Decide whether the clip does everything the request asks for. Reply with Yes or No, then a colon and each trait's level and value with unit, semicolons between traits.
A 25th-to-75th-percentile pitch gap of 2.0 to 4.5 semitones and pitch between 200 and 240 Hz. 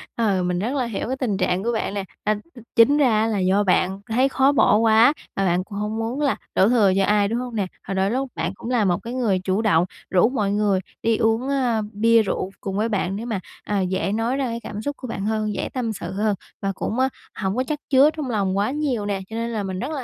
Yes: average, 3.8 semitones; high, 220 Hz